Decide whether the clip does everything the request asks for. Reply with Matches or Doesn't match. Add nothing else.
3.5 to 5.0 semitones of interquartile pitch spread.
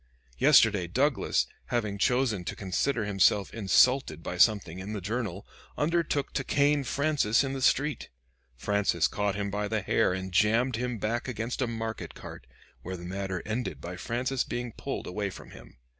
Matches